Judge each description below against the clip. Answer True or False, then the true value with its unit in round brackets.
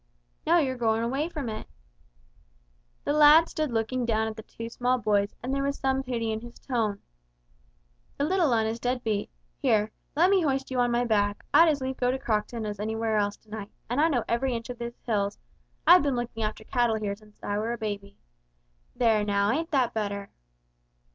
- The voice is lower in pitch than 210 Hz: False (235 Hz)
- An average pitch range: True (3.6 semitones)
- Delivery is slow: False (205 wpm)